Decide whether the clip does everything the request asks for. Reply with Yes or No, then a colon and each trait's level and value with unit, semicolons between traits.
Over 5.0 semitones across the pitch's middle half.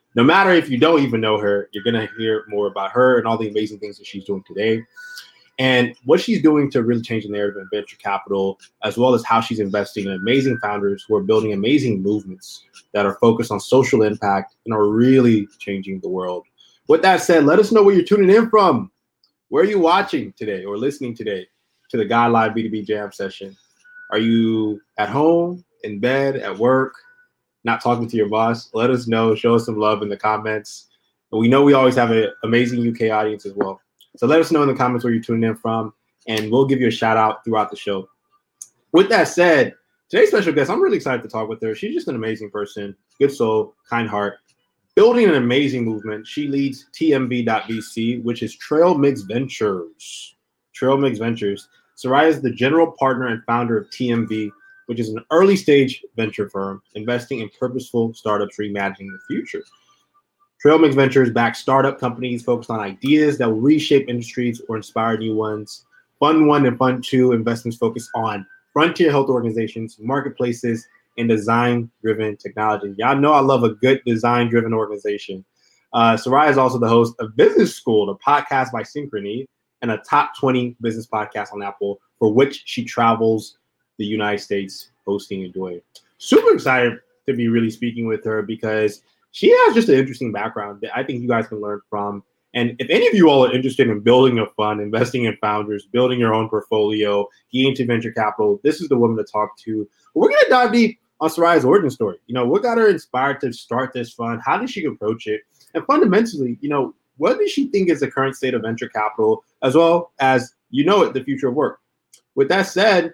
No: average, 4.2 semitones